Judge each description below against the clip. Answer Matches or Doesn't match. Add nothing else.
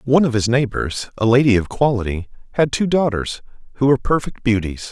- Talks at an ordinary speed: Matches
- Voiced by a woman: Doesn't match